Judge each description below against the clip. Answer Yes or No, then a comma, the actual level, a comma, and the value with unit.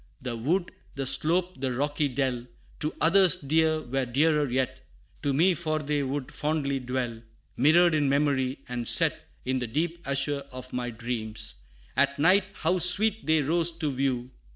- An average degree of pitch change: Yes, average, 3.8 semitones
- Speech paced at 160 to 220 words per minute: Yes, average, 165 wpm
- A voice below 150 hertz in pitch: Yes, medium, 140 Hz